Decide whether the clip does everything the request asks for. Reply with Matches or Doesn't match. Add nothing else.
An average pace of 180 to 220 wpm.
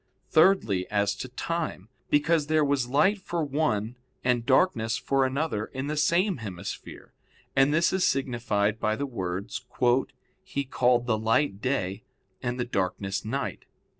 Doesn't match